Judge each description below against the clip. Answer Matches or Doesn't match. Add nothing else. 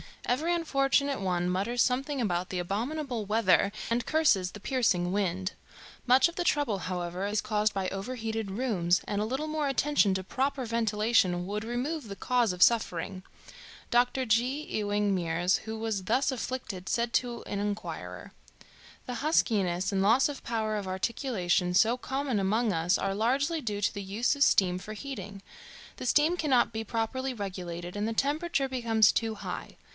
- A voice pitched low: Doesn't match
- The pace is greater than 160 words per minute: Matches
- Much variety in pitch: Doesn't match